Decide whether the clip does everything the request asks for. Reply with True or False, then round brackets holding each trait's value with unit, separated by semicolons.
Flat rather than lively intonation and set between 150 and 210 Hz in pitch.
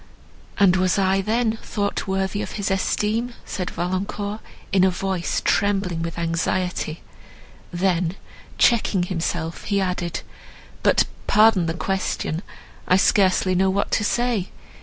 True (2.3 semitones; 190 Hz)